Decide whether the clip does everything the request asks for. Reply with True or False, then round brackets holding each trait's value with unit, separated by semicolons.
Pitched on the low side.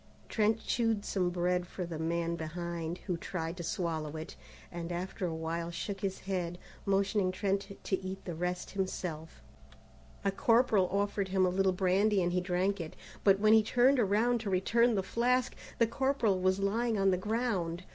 False (190 Hz)